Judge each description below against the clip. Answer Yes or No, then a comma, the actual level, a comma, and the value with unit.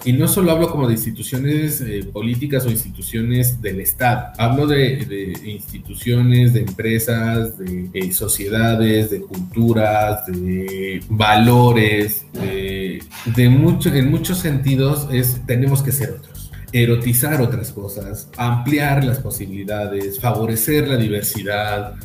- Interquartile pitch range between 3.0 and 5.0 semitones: Yes, average, 3.9 semitones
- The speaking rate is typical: No, slow, 120 wpm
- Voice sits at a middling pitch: No, low, 115 Hz